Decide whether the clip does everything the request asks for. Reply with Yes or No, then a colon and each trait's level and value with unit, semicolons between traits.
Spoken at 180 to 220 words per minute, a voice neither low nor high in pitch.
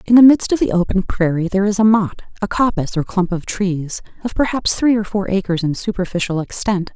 No: fast, 205 wpm; high, 200 Hz